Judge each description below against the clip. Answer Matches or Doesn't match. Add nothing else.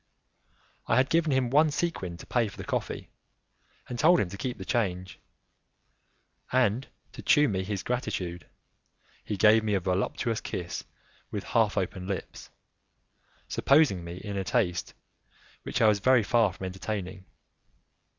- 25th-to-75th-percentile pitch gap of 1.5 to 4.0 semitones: Doesn't match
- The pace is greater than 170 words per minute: Doesn't match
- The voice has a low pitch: Matches